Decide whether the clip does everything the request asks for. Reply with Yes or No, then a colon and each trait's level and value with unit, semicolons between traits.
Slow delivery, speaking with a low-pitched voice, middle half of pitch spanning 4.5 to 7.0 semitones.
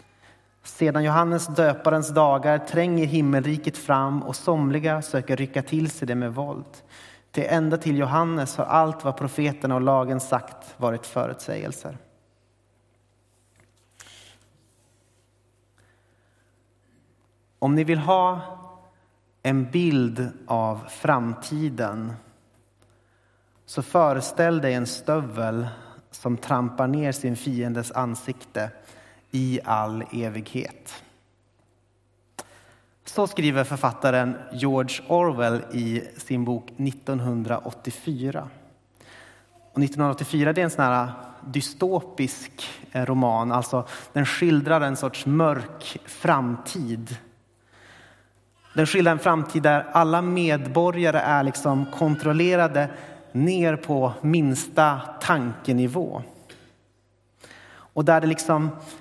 Yes: slow, 95 wpm; low, 130 Hz; average, 4.9 semitones